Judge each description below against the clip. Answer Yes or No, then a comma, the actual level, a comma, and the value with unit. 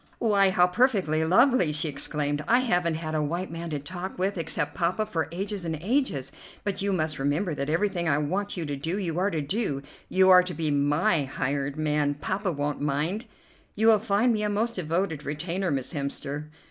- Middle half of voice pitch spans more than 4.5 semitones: Yes, average, 4.9 semitones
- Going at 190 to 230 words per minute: Yes, average, 200 wpm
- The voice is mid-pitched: Yes, medium, 170 Hz